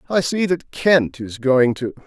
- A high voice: No, medium, 145 Hz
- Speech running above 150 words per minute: Yes, fast, 205 wpm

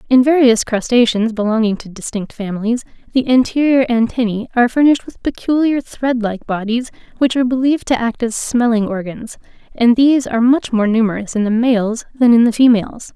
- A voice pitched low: No, high, 235 Hz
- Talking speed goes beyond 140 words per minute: Yes, average, 175 wpm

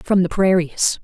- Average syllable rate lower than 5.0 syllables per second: Yes, 4.4 syllables/s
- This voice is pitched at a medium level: Yes, medium, 180 Hz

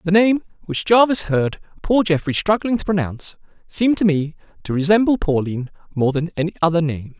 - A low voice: No, medium, 175 Hz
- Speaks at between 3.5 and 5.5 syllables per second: No, 5.8 syllables/s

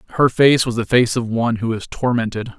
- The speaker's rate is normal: No, fast, 230 wpm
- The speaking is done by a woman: No, male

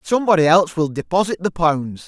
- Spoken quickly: No, average, 175 wpm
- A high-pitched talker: No, medium, 170 Hz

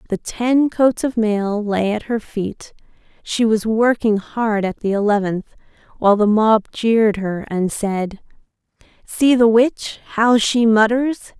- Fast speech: No, average, 155 wpm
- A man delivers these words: No, female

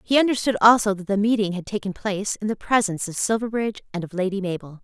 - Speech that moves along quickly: Yes, fast, 225 wpm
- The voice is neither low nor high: No, high, 205 Hz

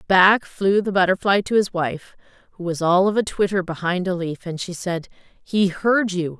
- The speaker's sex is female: Yes, female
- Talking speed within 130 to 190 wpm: No, fast, 205 wpm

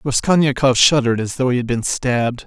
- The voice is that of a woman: No, male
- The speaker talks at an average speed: Yes, average, 195 wpm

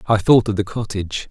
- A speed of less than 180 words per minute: No, fast, 230 wpm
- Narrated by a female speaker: No, male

